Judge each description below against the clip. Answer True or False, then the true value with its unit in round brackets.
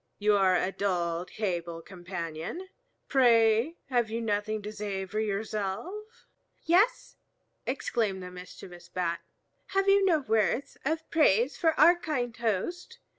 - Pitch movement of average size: False (8.2 semitones)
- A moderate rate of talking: False (130 wpm)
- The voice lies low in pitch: False (215 Hz)